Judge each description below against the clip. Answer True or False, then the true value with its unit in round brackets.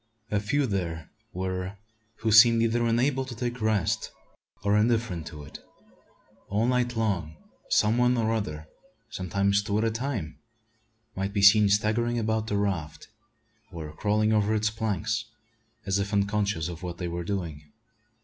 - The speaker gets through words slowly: False (155 wpm)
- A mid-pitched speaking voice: False (105 Hz)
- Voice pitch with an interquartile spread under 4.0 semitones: True (3.4 semitones)